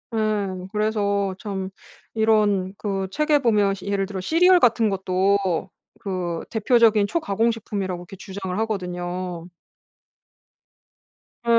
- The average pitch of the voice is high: Yes, high, 200 Hz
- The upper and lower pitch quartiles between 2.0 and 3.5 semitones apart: Yes, average, 2.7 semitones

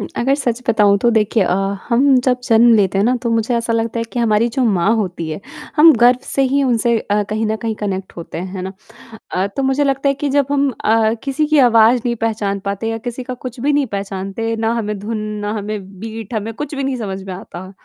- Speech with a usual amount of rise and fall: Yes, average, 3.5 semitones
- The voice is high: Yes, high, 225 Hz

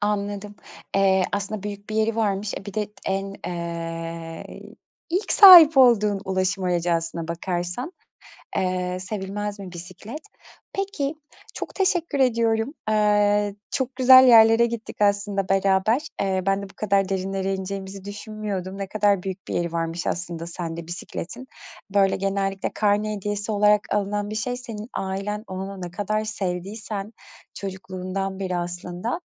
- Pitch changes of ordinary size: No, narrow, 2.3 semitones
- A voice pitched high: Yes, high, 200 Hz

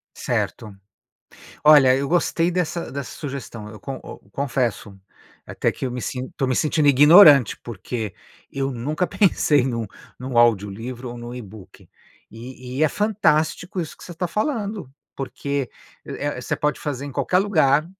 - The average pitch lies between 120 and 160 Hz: Yes, low, 135 Hz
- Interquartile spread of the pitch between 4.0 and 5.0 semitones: Yes, average, 4.5 semitones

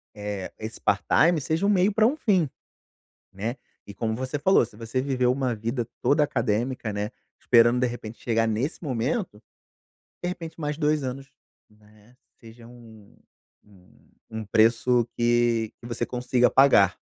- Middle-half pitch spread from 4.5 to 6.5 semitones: No, average, 3.8 semitones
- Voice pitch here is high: No, low, 120 Hz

